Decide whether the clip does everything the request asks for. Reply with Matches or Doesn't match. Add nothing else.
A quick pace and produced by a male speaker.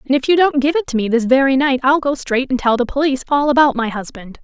Doesn't match